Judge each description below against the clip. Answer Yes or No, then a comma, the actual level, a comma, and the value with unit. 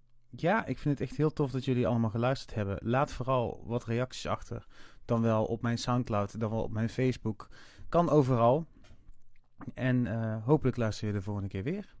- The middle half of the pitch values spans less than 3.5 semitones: Yes, narrow, 2.6 semitones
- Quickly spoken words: No, average, 190 wpm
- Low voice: Yes, low, 120 Hz